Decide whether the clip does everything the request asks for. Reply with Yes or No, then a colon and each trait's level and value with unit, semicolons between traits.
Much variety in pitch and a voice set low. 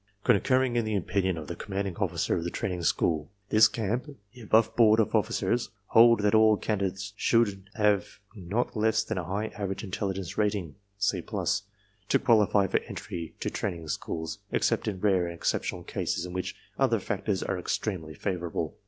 No: average, 3.0 semitones; low, 100 Hz